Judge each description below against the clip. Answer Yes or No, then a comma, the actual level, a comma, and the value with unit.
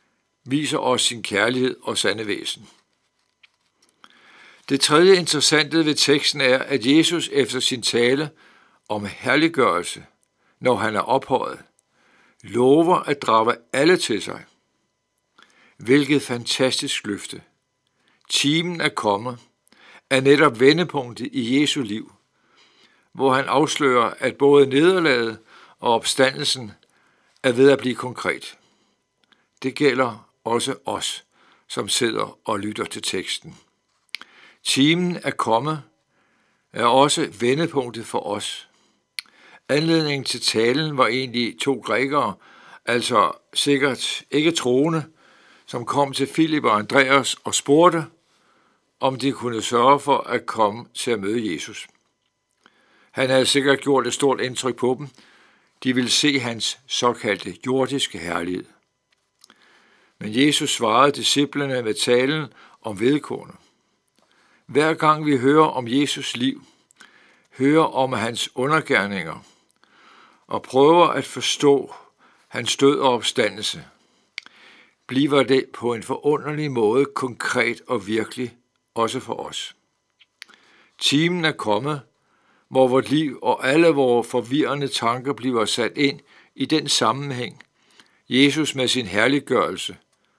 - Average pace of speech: No, slow, 120 wpm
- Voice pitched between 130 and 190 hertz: Yes, low, 135 Hz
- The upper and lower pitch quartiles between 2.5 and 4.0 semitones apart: Yes, average, 2.9 semitones